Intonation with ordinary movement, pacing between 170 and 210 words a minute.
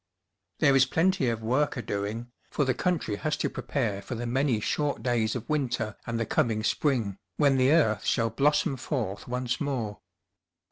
Yes: average, 4.2 semitones; average, 180 wpm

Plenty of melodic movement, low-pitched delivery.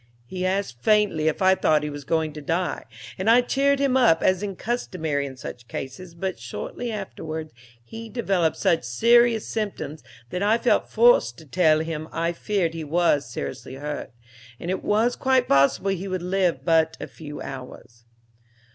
No: wide, 5.7 semitones; medium, 170 Hz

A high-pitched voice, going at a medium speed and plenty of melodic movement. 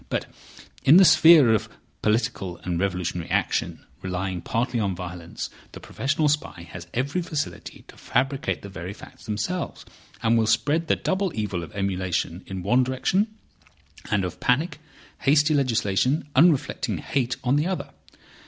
No: low, 115 Hz; average, 150 wpm; wide, 7.6 semitones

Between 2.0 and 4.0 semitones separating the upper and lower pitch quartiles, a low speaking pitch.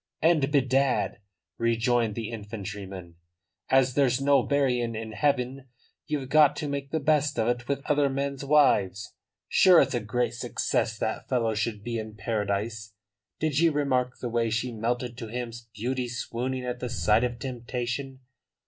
Yes: average, 3.3 semitones; low, 125 Hz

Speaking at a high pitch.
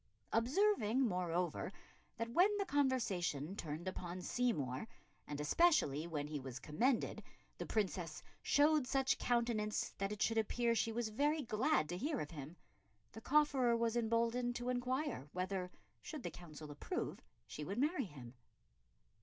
Yes: high, 220 Hz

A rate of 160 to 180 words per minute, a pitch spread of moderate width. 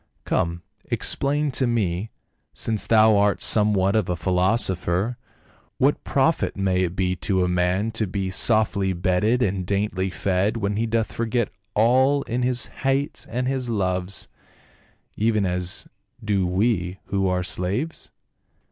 No: average, 145 wpm; average, 3.9 semitones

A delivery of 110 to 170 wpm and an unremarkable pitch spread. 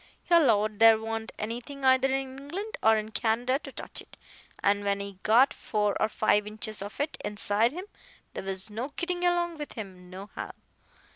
No: average, 185 wpm; average, 4.7 semitones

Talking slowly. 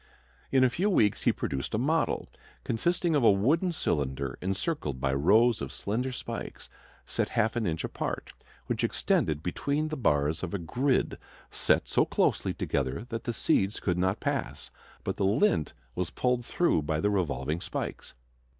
No: average, 170 wpm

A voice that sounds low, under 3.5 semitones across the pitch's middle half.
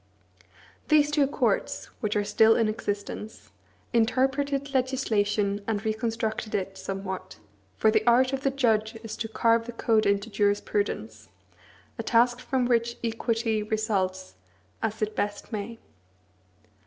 No: high, 220 Hz; narrow, 2.6 semitones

